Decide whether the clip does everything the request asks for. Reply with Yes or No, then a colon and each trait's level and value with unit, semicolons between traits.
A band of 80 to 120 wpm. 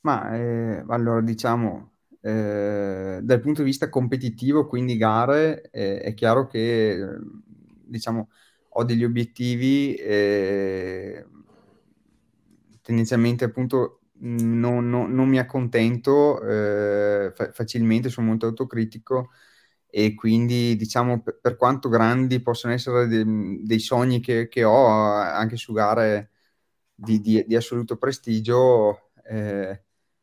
Yes: slow, 115 wpm